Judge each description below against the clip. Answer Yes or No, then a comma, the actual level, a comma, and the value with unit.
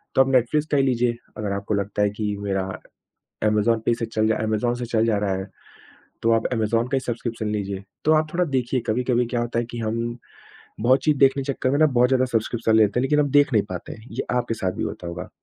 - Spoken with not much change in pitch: No, average, 3.3 semitones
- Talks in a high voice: No, low, 115 Hz